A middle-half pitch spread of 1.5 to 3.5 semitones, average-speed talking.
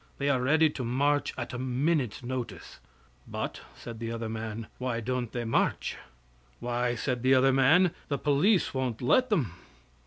Yes: average, 3.1 semitones; average, 165 wpm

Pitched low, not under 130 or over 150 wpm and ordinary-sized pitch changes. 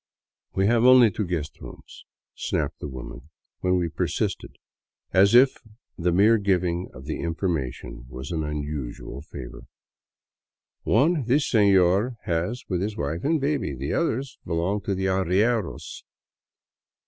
No: very low, 90 Hz; average, 145 wpm; wide, 6.2 semitones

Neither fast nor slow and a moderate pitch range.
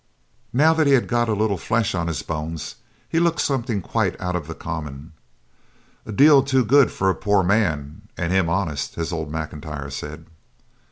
No: average, 185 wpm; wide, 7.0 semitones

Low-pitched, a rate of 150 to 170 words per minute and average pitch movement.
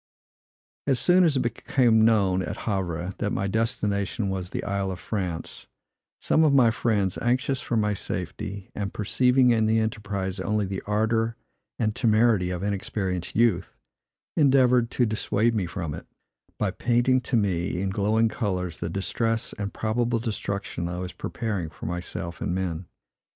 Yes: low, 105 Hz; average, 160 wpm; average, 3.6 semitones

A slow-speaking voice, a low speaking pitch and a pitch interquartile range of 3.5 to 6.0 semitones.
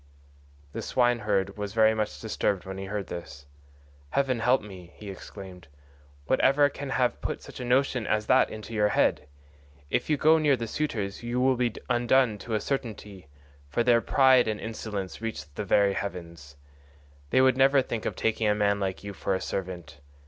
No: average, 185 wpm; low, 110 Hz; average, 4.2 semitones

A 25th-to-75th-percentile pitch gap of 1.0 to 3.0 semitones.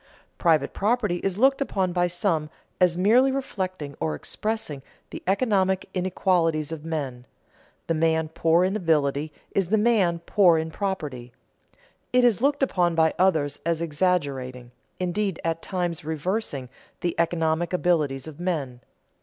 No: average, 3.5 semitones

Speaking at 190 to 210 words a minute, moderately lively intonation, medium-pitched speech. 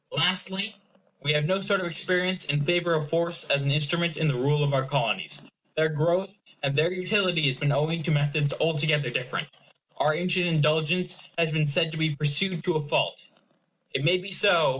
Yes: average, 195 wpm; average, 3.4 semitones; medium, 160 Hz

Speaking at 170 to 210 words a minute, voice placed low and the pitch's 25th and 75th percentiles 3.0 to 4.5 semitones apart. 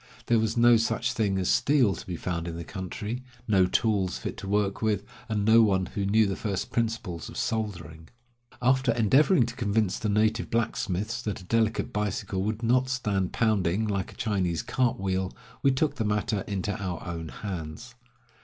Yes: average, 185 wpm; low, 105 Hz; average, 3.3 semitones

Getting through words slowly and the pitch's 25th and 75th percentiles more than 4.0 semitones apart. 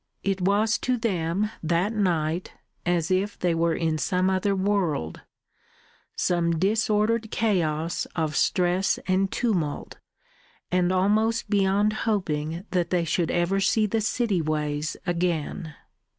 No: slow, 125 wpm; average, 3.7 semitones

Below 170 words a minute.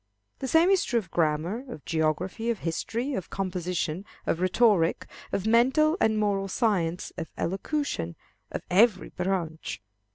Yes: average, 140 wpm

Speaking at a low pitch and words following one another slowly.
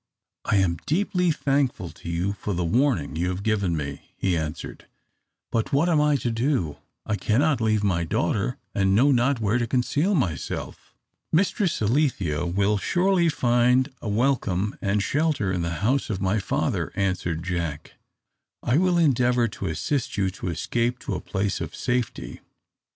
No: low, 110 Hz; average, 165 wpm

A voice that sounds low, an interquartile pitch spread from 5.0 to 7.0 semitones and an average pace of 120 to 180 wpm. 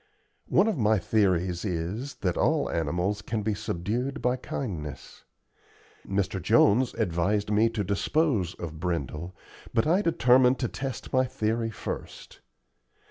Yes: low, 105 Hz; wide, 5.6 semitones; slow, 135 wpm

